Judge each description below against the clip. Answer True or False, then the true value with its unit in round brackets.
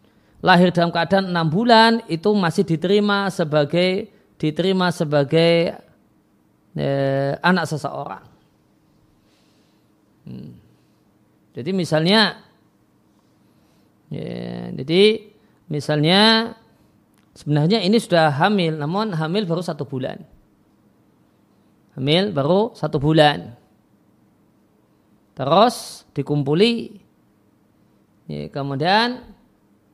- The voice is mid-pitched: True (160 Hz)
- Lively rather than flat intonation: True (6.8 semitones)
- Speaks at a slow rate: True (75 wpm)